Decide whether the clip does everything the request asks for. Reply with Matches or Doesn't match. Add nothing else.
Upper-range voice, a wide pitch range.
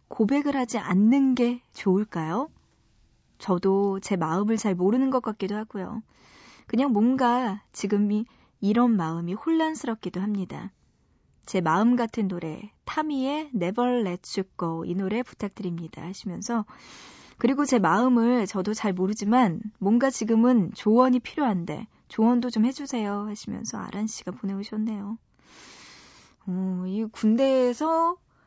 Doesn't match